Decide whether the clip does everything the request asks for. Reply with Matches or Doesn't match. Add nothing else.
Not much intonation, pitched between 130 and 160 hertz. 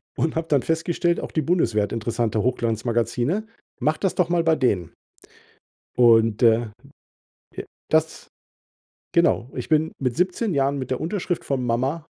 Doesn't match